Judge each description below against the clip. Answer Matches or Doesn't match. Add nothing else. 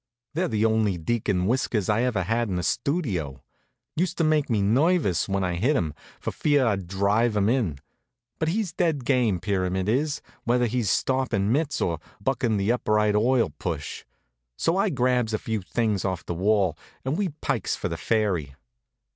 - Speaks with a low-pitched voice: Matches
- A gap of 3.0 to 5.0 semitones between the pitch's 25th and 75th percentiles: Doesn't match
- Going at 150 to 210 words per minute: Matches